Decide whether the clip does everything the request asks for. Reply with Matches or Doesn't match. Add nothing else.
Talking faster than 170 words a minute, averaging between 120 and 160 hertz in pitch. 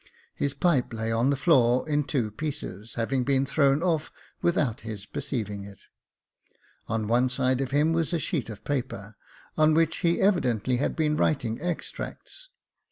Doesn't match